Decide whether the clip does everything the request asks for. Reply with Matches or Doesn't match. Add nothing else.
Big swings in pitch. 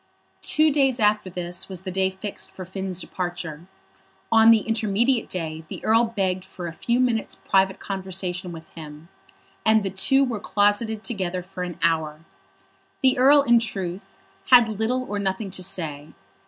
Doesn't match